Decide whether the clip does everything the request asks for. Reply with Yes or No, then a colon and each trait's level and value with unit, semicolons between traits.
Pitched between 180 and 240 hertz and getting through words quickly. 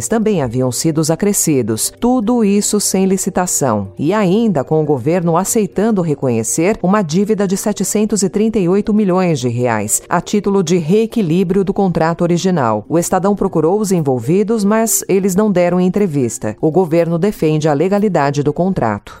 No: medium, 185 Hz; average, 145 wpm